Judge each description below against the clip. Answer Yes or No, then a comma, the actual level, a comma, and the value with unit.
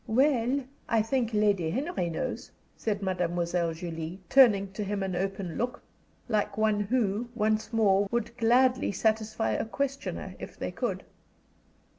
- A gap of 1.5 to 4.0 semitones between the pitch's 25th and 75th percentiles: Yes, average, 3.6 semitones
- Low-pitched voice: No, high, 215 Hz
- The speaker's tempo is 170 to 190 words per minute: No, average, 140 wpm